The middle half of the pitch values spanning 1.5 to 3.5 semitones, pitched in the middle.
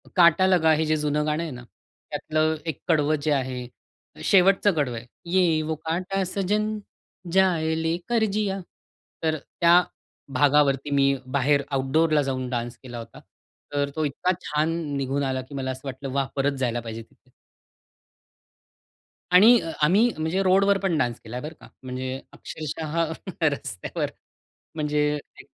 No: average, 4.2 semitones; medium, 150 Hz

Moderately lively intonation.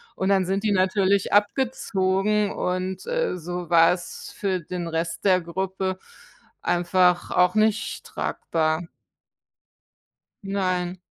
No: narrow, 2.0 semitones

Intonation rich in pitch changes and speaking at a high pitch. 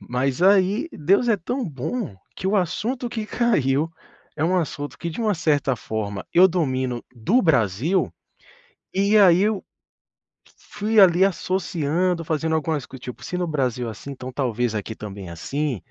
No: wide, 6.8 semitones; medium, 160 Hz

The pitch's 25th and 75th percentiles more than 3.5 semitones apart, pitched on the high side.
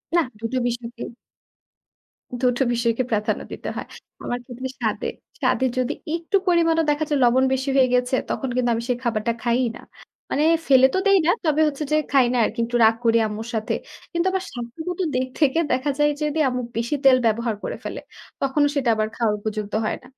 Yes: average, 4.0 semitones; very high, 255 Hz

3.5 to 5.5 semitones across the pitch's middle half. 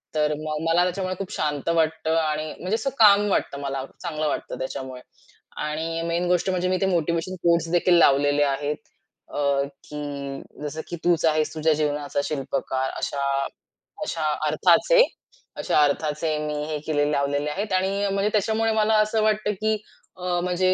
Yes: average, 3.9 semitones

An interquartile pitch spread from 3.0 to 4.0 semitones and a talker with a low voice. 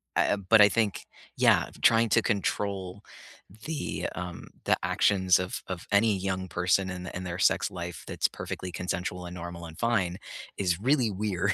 No: narrow, 2.5 semitones; very low, 95 Hz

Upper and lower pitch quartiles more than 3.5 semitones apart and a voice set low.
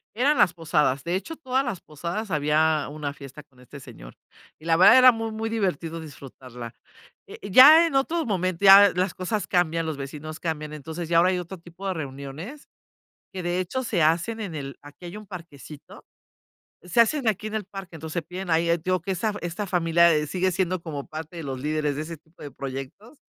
No: average, 4.4 semitones; medium, 170 Hz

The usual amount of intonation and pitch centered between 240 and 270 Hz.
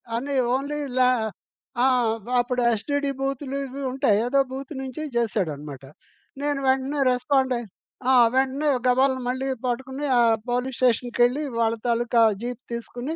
No: narrow, 2.1 semitones; very high, 260 Hz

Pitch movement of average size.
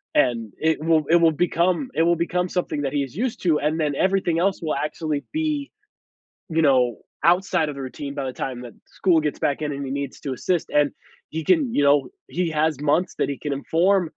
Yes: average, 3.8 semitones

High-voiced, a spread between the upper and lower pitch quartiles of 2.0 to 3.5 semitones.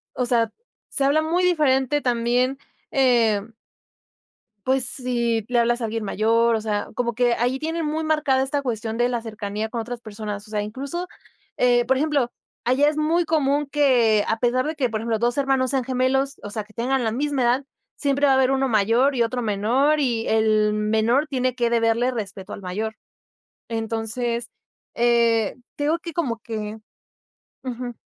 Yes: high, 240 Hz; average, 3.2 semitones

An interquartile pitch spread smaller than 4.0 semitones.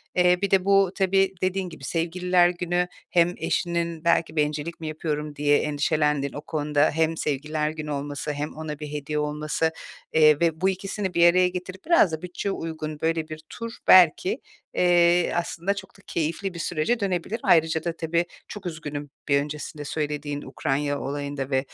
Yes: average, 3.0 semitones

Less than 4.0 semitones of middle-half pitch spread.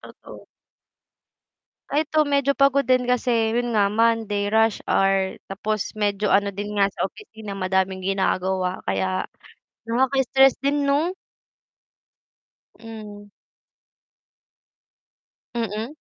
No: average, 4.3 semitones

